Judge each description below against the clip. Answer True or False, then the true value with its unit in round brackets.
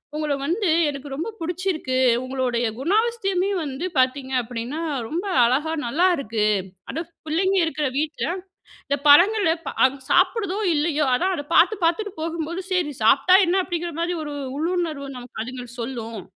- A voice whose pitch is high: True (310 Hz)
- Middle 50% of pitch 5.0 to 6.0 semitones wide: True (5.3 semitones)